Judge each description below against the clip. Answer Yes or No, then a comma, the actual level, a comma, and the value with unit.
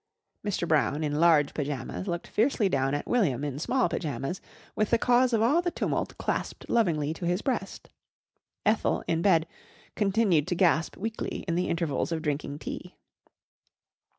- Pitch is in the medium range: Yes, medium, 170 Hz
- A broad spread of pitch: Yes, wide, 6.2 semitones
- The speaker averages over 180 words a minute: No, average, 160 wpm